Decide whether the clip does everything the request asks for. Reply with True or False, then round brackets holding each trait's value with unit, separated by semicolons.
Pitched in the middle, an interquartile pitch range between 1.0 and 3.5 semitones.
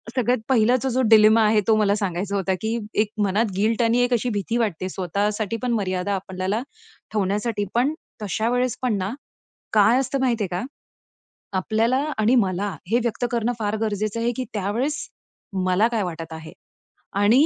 False (215 Hz; 3.0 semitones)